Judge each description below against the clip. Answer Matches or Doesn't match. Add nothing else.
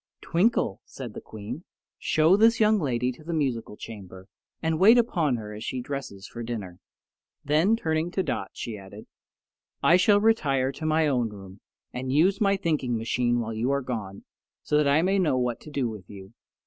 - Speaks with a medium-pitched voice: Doesn't match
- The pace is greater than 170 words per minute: Matches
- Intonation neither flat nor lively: Doesn't match